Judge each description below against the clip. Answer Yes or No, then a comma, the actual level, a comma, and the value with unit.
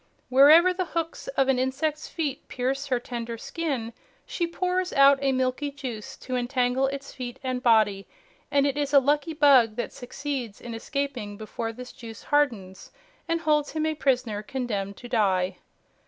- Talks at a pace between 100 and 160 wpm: No, average, 170 wpm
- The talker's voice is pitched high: Yes, very high, 265 Hz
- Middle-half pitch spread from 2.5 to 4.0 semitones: Yes, average, 3.6 semitones